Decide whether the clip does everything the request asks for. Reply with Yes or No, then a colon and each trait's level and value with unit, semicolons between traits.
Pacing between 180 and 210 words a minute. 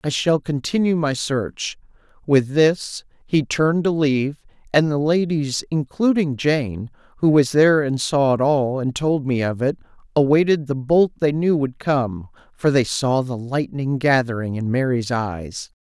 No: average, 165 wpm